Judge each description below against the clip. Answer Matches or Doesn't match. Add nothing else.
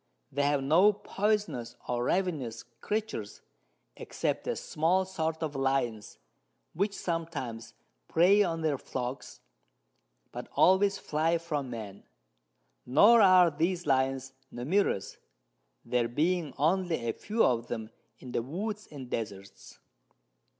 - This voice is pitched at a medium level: Matches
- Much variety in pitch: Matches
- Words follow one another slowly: Matches